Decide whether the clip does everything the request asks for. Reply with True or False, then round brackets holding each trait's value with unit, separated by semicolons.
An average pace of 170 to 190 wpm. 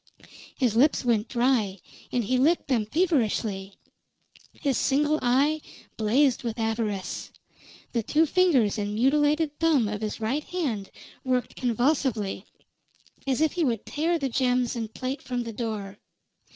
False (140 wpm)